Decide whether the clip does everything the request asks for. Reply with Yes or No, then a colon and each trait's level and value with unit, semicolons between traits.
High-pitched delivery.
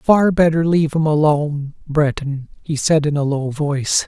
No: medium, 150 Hz